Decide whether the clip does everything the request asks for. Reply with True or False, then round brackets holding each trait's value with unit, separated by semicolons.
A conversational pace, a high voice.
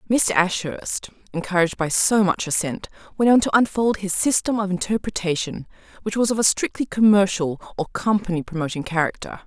True (160 wpm; 195 Hz)